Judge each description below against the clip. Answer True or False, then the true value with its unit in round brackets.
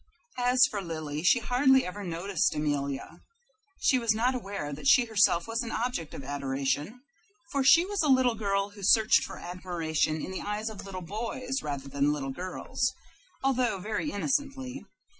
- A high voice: True (205 Hz)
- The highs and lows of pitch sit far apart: True (7.6 semitones)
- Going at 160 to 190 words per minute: True (170 wpm)